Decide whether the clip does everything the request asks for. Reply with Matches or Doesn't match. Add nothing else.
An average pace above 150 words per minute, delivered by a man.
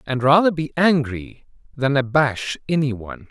Doesn't match